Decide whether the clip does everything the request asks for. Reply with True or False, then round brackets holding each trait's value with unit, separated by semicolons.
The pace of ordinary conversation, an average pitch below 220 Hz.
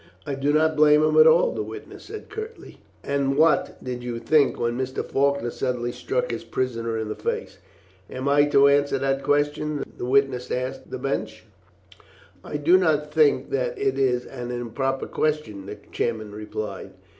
True (175 wpm; 140 Hz)